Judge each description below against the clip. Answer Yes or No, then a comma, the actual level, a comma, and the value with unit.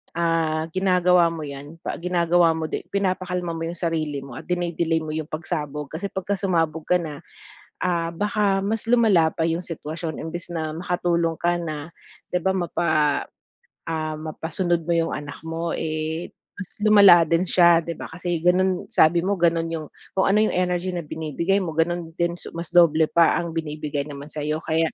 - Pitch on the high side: No, medium, 170 Hz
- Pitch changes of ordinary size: No, narrow, 2.1 semitones